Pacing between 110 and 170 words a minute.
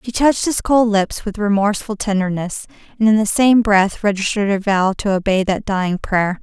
No: average, 195 wpm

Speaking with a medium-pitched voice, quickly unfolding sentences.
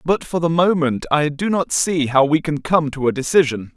Yes: medium, 155 Hz; fast, 240 wpm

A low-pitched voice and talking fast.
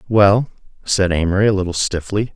No: low, 100 Hz; average, 155 wpm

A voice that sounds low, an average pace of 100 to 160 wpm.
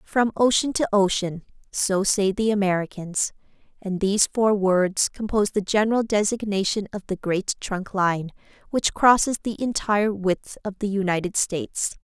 No: high, 200 Hz; average, 145 wpm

